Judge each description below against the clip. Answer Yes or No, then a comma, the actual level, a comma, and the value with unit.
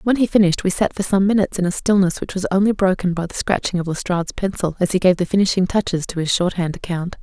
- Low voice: No, medium, 185 Hz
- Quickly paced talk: Yes, fast, 255 wpm